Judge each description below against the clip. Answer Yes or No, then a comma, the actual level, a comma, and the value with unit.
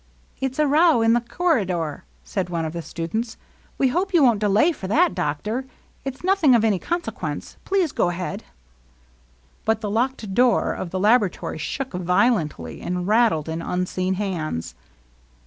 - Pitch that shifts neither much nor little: No, wide, 6.6 semitones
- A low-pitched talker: No, high, 215 Hz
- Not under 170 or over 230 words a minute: Yes, average, 180 wpm